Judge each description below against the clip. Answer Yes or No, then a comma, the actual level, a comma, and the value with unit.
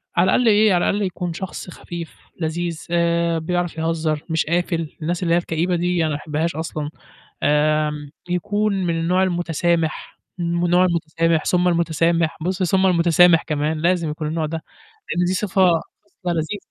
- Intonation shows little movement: Yes, narrow, 1.8 semitones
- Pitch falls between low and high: Yes, medium, 170 Hz